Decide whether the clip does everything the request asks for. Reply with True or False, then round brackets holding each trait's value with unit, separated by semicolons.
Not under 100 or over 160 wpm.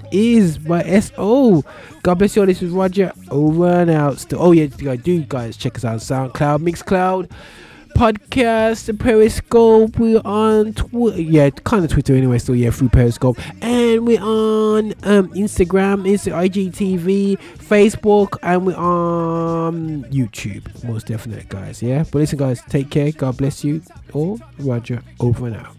True (155 wpm)